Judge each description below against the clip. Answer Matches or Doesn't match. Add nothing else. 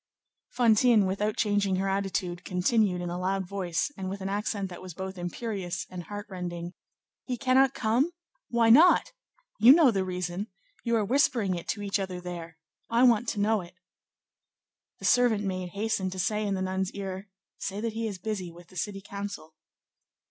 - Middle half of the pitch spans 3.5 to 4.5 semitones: Doesn't match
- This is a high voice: Matches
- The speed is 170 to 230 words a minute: Matches